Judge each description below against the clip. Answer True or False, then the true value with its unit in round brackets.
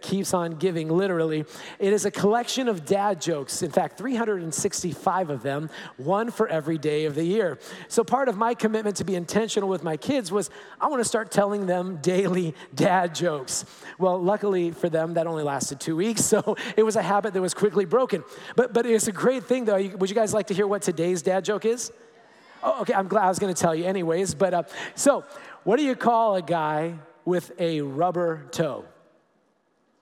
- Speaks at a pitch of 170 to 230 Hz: True (190 Hz)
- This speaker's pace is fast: True (210 wpm)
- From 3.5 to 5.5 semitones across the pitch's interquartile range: True (4.1 semitones)